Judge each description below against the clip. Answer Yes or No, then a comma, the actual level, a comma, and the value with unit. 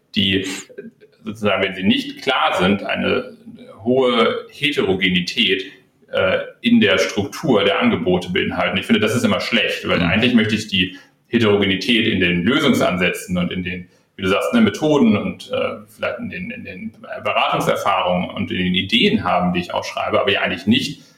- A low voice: Yes, low, 115 Hz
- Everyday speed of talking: Yes, average, 170 wpm